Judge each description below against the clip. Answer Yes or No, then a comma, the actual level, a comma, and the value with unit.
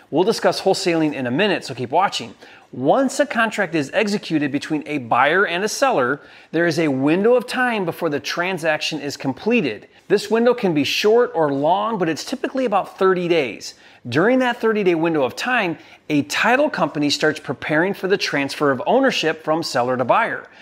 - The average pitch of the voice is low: No, medium, 170 Hz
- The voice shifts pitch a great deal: Yes, wide, 6.5 semitones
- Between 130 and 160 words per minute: No, average, 190 wpm